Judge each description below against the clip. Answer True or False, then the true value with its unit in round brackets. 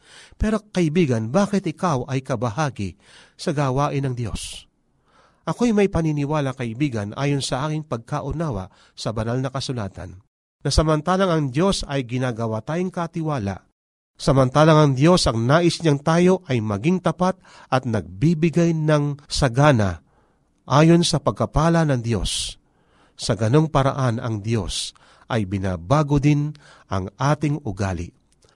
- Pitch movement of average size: False (6.1 semitones)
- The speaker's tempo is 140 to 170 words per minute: False (125 wpm)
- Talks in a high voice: False (140 Hz)